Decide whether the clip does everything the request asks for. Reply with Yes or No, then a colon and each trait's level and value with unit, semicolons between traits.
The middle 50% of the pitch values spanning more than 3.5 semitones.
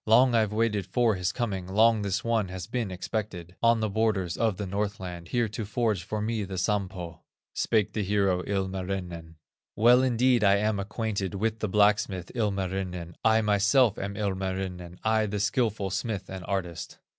No: average, 2.8 semitones